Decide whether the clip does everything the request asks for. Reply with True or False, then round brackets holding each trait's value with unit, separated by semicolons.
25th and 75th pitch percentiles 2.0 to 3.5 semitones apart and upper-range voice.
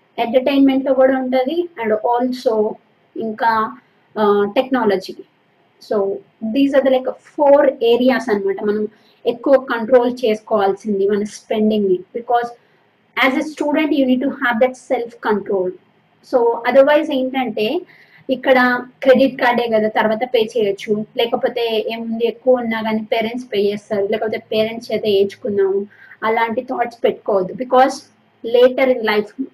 True (3.2 semitones; 235 Hz)